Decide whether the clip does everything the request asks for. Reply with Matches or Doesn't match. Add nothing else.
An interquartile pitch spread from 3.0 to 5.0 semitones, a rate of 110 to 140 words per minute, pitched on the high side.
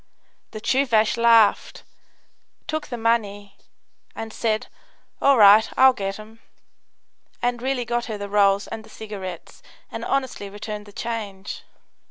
Doesn't match